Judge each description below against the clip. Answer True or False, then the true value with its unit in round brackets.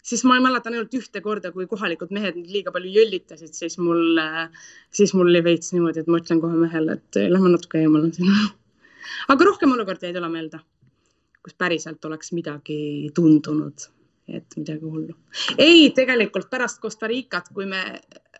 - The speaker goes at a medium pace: True (165 wpm)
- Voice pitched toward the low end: False (180 Hz)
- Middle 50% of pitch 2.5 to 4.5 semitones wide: False (5.4 semitones)